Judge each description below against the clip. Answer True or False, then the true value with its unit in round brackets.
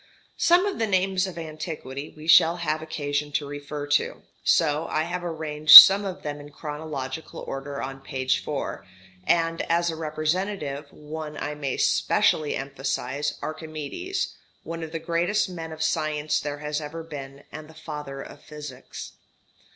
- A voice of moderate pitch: True (155 Hz)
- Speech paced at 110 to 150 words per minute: False (160 wpm)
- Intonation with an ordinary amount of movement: False (2.2 semitones)